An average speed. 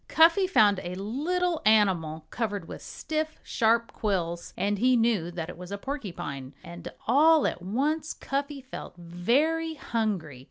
Yes: average, 150 wpm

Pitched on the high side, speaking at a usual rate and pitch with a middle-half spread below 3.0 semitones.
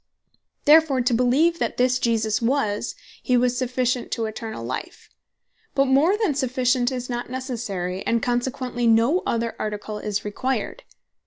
Yes: high, 245 Hz; average, 145 wpm; narrow, 2.5 semitones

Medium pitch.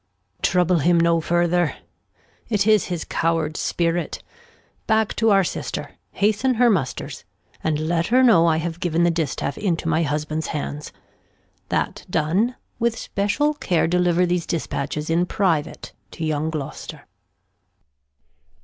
Yes: medium, 170 Hz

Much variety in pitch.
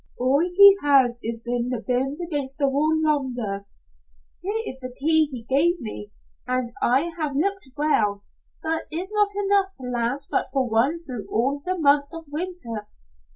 No: average, 5.0 semitones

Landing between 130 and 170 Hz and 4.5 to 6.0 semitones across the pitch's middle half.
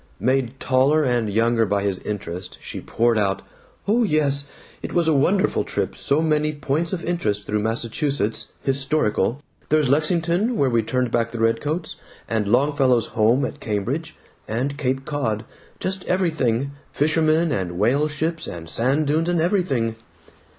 Yes: low, 135 Hz; average, 5.3 semitones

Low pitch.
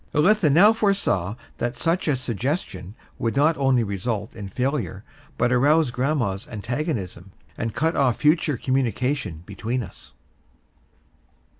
Yes: low, 125 Hz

